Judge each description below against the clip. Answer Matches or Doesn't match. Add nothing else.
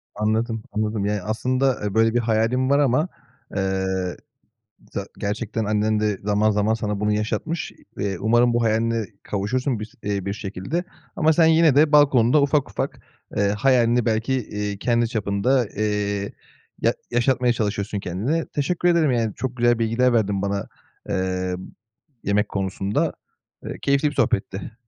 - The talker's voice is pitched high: Doesn't match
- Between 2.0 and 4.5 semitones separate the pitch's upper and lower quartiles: Matches